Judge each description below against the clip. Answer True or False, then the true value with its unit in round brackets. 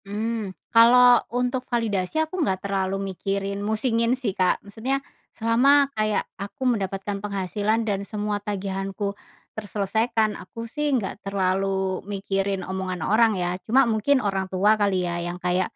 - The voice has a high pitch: True (205 Hz)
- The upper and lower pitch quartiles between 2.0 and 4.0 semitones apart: True (3.1 semitones)